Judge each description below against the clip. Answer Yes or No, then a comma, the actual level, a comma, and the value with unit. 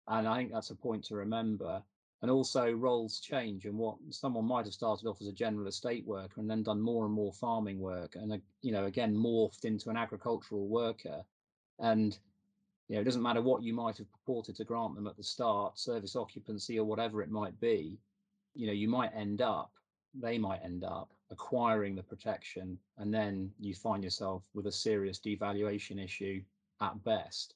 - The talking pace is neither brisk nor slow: Yes, average, 195 wpm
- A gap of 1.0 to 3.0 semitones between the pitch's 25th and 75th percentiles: Yes, narrow, 2.4 semitones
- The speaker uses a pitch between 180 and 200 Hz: No, low, 105 Hz